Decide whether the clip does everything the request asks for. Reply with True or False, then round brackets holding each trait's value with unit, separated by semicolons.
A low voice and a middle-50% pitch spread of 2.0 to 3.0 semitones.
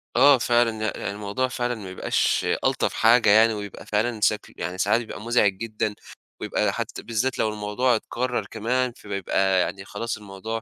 True (110 Hz; 2.7 semitones)